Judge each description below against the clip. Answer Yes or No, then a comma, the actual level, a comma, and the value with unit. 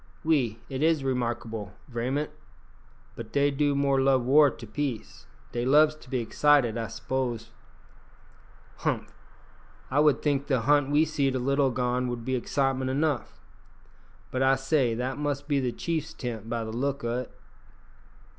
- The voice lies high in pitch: No, low, 130 Hz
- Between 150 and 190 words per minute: Yes, average, 160 wpm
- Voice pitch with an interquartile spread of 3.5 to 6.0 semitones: No, average, 3.0 semitones